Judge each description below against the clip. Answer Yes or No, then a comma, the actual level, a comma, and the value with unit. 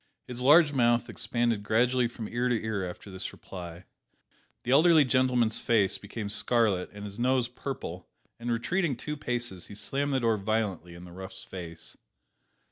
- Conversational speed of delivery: Yes, average, 165 wpm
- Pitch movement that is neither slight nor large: Yes, average, 4.3 semitones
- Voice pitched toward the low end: Yes, low, 115 Hz